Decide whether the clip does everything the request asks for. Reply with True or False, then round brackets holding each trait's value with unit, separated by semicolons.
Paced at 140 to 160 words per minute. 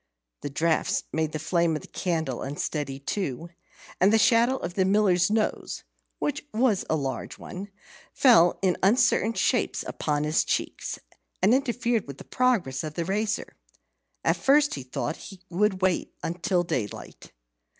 True (155 wpm)